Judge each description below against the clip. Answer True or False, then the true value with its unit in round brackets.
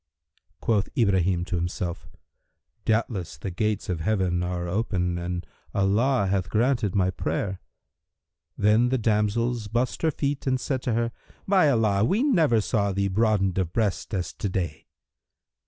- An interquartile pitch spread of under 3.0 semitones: False (4.2 semitones)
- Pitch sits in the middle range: False (105 Hz)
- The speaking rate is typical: True (150 wpm)